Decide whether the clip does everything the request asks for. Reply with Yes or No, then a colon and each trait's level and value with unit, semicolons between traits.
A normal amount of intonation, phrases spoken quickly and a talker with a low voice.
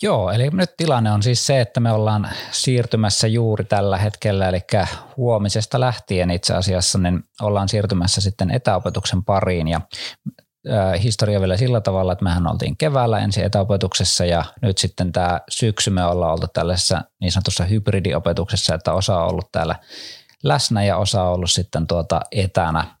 Yes: average, 3.2 semitones; fast, 160 wpm; low, 100 Hz